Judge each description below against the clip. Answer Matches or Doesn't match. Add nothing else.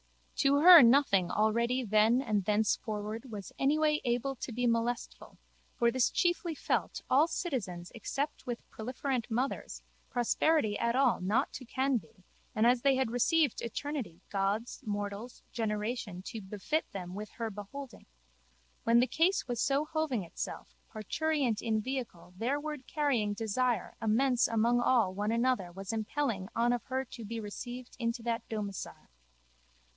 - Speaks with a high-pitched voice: Matches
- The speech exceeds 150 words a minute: Doesn't match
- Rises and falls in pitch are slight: Doesn't match